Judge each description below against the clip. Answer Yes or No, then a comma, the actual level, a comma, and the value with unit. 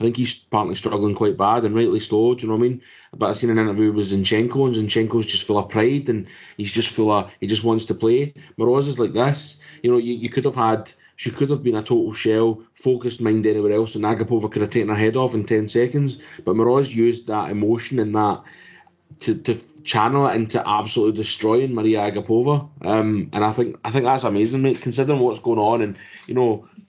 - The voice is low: Yes, low, 115 Hz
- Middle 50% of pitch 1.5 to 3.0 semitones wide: Yes, narrow, 2.4 semitones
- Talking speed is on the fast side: Yes, fast, 230 wpm